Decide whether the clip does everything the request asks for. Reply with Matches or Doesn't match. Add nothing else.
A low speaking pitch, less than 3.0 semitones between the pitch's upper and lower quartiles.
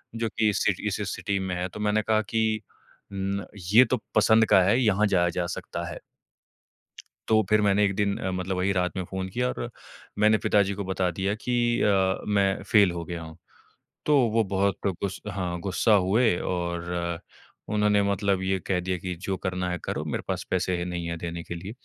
Matches